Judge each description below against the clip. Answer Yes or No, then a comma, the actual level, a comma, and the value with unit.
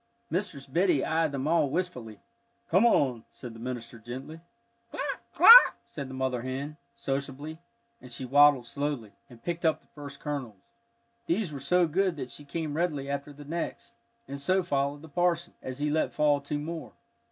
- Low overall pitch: No, medium, 145 Hz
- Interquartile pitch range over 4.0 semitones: No, average, 3.7 semitones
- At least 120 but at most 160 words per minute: No, average, 175 wpm